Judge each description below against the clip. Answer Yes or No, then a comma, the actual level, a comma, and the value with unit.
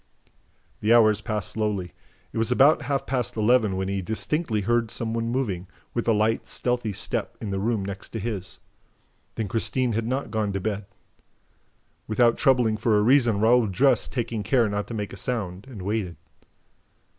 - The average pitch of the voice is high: No, low, 110 Hz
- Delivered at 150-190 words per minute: Yes, average, 180 wpm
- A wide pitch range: No, average, 2.8 semitones